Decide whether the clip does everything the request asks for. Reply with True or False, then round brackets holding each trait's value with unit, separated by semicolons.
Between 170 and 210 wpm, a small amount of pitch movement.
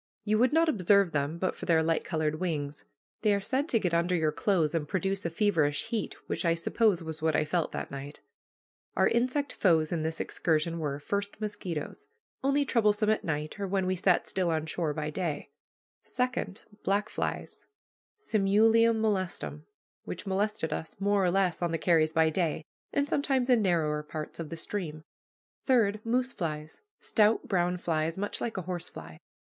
False (180 wpm; 4.8 semitones)